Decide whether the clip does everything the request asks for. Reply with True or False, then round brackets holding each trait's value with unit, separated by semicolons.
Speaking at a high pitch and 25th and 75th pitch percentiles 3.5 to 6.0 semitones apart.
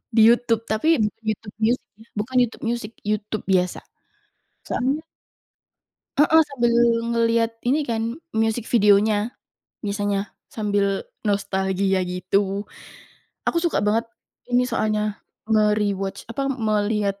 False (215 Hz; 2.8 semitones)